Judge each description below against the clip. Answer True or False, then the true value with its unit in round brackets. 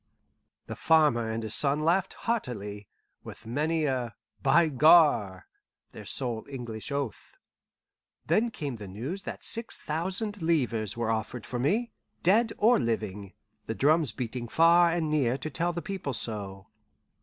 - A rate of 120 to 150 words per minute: True (145 wpm)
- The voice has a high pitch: False (140 Hz)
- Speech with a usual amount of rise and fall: False (6.9 semitones)